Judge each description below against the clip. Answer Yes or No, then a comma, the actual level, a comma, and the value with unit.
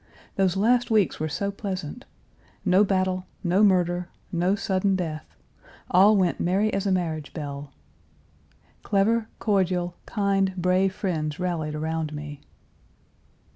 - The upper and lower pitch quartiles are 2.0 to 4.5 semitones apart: Yes, average, 3.3 semitones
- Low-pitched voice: No, medium, 185 Hz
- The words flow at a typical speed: No, slow, 125 wpm